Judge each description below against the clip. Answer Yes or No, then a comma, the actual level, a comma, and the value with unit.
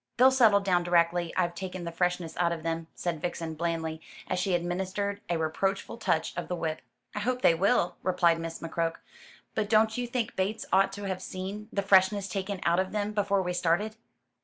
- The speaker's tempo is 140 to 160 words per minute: No, average, 200 wpm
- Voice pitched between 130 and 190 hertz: Yes, medium, 185 Hz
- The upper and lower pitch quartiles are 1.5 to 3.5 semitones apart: Yes, average, 3.0 semitones